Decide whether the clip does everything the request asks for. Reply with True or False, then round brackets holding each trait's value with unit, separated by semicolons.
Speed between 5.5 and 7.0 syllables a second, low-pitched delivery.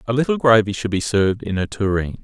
True (6.3 syllables/s; 110 Hz)